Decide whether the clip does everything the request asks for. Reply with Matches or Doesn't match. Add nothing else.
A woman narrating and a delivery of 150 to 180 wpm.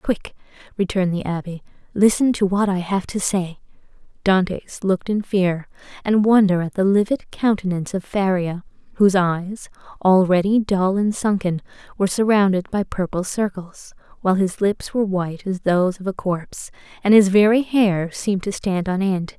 Matches